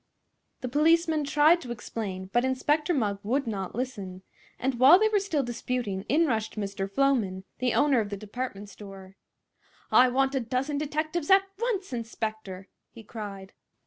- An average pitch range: No, wide, 6.4 semitones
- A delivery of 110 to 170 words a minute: Yes, average, 160 wpm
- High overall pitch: Yes, high, 245 Hz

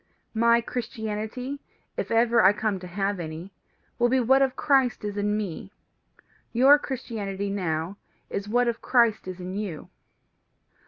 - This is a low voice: No, high, 215 Hz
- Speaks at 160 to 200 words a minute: No, average, 150 wpm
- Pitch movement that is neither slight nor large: Yes, average, 3.6 semitones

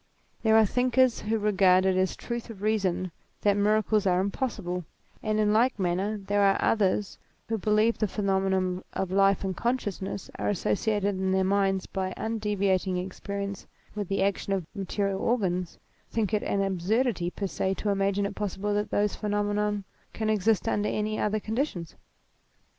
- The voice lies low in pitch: No, high, 200 Hz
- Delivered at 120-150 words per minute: No, average, 170 wpm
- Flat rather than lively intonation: Yes, narrow, 2.0 semitones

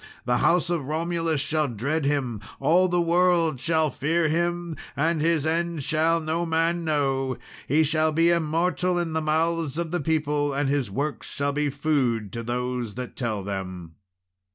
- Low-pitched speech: No, medium, 155 Hz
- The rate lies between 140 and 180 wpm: Yes, average, 170 wpm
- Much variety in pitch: No, average, 3.6 semitones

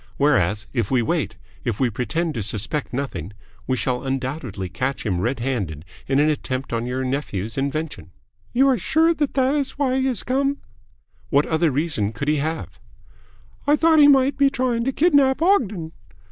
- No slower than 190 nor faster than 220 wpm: No, average, 180 wpm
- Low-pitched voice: No, medium, 145 Hz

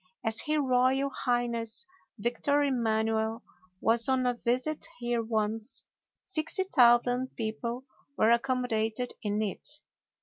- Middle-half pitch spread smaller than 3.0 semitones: Yes, narrow, 2.6 semitones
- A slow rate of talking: Yes, slow, 105 wpm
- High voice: Yes, high, 240 Hz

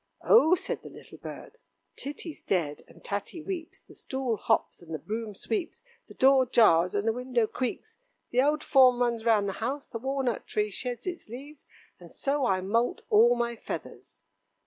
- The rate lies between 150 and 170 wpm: No, average, 180 wpm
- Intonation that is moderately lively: Yes, average, 4.2 semitones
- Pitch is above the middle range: Yes, high, 240 Hz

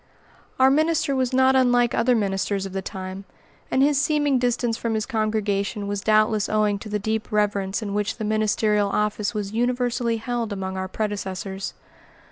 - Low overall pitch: No, high, 215 Hz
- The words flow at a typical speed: Yes, average, 170 wpm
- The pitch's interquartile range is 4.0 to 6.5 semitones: No, average, 3.3 semitones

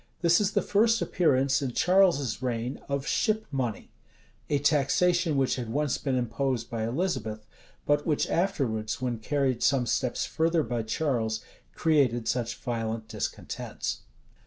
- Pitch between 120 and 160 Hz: Yes, low, 135 Hz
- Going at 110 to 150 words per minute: Yes, average, 140 wpm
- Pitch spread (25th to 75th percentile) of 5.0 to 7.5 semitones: Yes, wide, 5.4 semitones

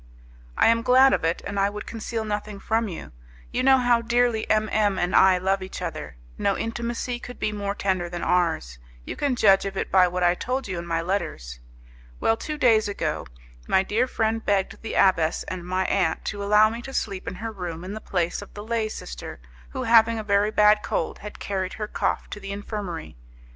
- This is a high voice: Yes, high, 205 Hz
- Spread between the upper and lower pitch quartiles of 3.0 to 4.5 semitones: Yes, average, 3.4 semitones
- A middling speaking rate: No, fast, 215 wpm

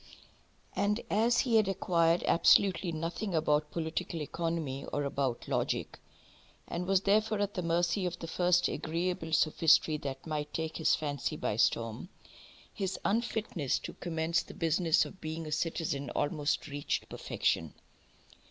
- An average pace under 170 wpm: Yes, average, 145 wpm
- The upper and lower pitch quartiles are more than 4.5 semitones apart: No, average, 3.1 semitones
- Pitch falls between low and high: Yes, medium, 165 Hz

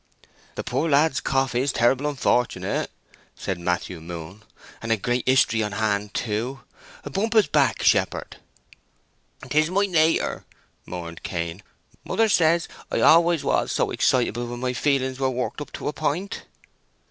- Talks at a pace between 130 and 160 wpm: Yes, average, 145 wpm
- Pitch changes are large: Yes, wide, 6.5 semitones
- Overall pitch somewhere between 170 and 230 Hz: No, low, 130 Hz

